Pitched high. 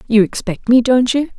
Yes: high, 235 Hz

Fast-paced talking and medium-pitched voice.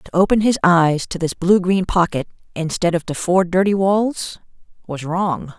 No: average, 185 wpm; medium, 180 Hz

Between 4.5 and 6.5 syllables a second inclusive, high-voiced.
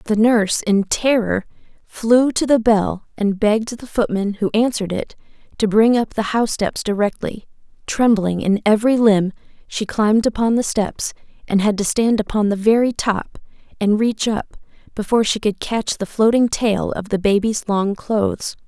Yes: 4.8 syllables/s; high, 215 Hz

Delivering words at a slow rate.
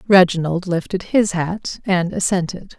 Yes: slow, 130 wpm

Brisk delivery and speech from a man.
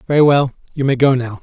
Yes: fast, 250 wpm; male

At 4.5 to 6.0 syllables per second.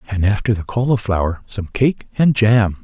Yes: 5.0 syllables/s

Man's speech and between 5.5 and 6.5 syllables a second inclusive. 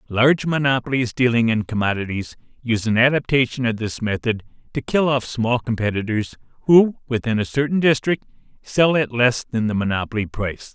Yes: male; 5.6 syllables/s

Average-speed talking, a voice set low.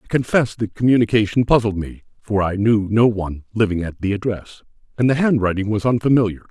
Yes: average, 185 wpm; low, 110 Hz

